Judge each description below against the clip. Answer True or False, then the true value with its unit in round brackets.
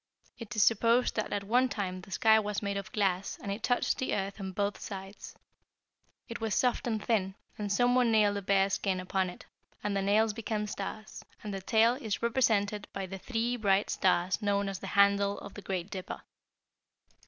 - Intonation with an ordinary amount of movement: False (2.3 semitones)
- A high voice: True (205 Hz)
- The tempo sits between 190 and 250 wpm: True (200 wpm)